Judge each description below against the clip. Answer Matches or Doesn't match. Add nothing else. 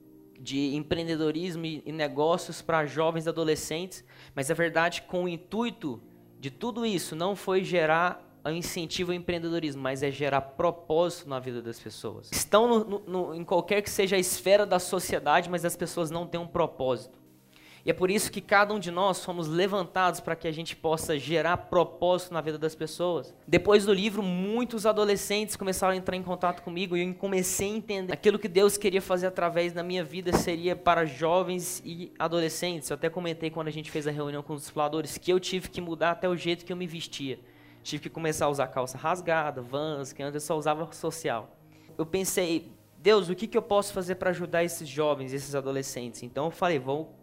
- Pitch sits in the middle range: Matches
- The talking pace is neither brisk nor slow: Doesn't match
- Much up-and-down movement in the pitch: Doesn't match